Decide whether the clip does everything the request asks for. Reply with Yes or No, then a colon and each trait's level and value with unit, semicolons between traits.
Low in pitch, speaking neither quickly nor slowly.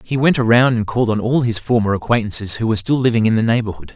No: low, 115 Hz; fast, 260 wpm